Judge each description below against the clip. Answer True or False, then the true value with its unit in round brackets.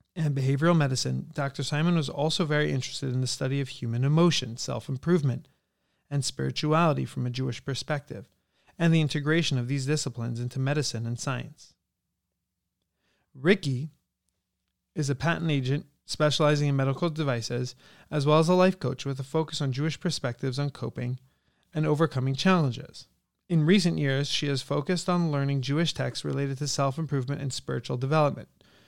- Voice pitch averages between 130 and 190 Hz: True (140 Hz)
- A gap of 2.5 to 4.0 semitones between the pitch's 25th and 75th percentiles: True (3.2 semitones)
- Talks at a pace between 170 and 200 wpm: False (160 wpm)